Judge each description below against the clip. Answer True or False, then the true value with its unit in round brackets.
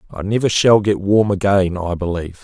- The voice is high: False (95 Hz)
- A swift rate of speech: False (195 wpm)